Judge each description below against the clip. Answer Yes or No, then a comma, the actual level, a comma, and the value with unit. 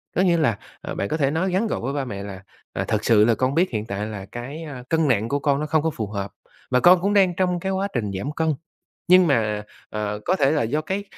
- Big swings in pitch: Yes, wide, 7.7 semitones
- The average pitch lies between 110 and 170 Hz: Yes, medium, 140 Hz